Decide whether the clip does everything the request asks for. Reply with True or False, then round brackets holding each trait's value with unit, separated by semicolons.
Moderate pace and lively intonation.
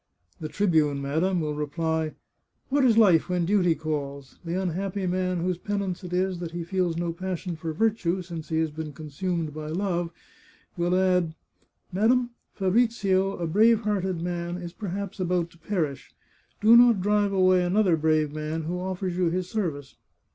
False (180 wpm; 3.0 semitones)